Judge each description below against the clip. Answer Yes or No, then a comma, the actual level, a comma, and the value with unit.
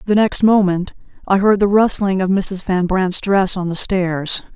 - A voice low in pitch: No, high, 190 Hz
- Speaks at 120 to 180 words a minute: No, average, 200 wpm